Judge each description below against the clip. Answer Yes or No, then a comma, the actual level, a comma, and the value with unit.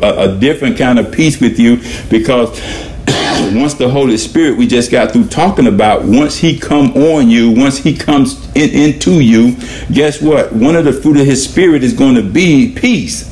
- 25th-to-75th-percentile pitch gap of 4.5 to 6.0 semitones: Yes, average, 5.0 semitones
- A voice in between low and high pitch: Yes, medium, 145 Hz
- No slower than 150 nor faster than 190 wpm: Yes, average, 185 wpm